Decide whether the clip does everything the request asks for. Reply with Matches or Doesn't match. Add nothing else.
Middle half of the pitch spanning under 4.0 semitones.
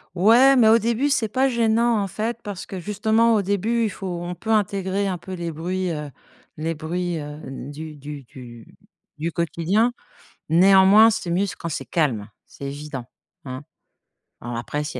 Doesn't match